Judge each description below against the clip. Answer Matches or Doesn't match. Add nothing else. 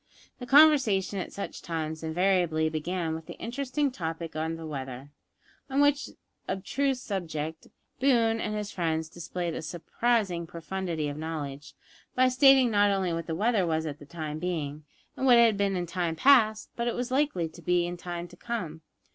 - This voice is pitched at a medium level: Matches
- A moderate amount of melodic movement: Doesn't match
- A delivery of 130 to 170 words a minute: Doesn't match